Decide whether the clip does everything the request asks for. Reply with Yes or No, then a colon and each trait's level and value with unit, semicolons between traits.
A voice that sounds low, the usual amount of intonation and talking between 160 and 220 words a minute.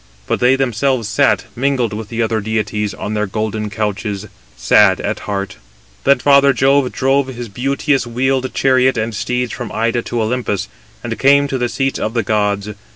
Yes: low, 120 Hz; average, 3.7 semitones; average, 175 wpm